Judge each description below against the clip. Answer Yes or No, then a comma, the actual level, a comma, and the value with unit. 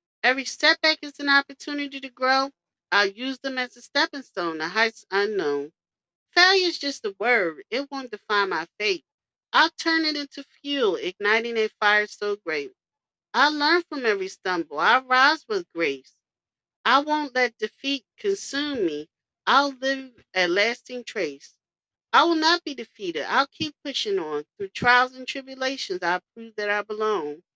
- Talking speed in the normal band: Yes, average, 165 wpm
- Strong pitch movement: Yes, wide, 6.1 semitones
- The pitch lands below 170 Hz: No, very high, 265 Hz